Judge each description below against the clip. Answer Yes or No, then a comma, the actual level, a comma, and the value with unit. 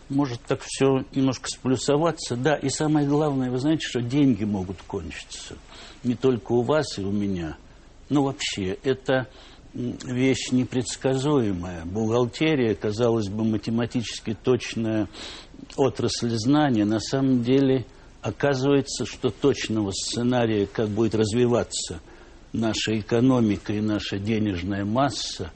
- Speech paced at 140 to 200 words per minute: No, average, 115 wpm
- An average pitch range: Yes, average, 3.9 semitones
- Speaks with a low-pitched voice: Yes, low, 120 Hz